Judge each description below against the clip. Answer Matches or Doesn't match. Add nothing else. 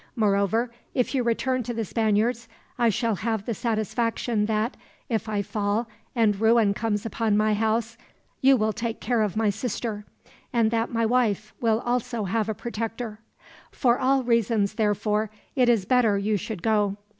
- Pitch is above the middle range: Matches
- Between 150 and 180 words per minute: Matches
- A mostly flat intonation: Matches